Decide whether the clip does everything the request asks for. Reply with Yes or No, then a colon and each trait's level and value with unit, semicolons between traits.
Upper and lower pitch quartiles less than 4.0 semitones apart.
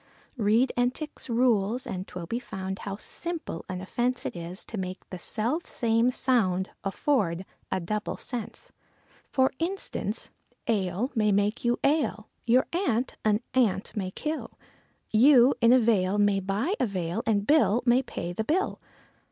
No: average, 4.8 semitones